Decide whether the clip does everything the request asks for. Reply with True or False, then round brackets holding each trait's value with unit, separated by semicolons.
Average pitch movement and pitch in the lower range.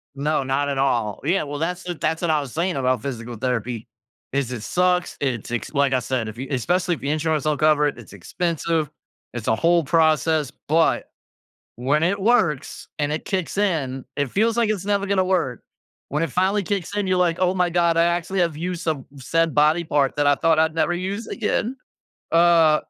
False (4.4 semitones; 160 Hz)